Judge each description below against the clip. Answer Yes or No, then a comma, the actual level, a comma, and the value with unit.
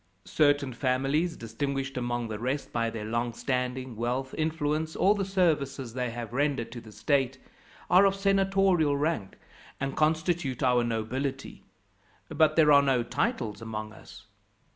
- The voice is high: No, low, 135 Hz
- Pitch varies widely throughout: No, average, 4.5 semitones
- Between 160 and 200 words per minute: No, average, 145 wpm